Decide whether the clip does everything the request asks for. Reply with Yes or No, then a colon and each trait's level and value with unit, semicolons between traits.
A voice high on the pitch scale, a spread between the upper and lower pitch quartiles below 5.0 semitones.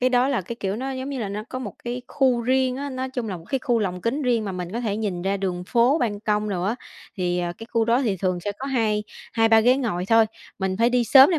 Yes: high, 225 Hz; average, 4.4 semitones